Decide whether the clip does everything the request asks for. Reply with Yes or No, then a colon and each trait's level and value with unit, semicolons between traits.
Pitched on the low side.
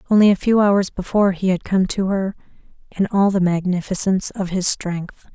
No: high, 190 Hz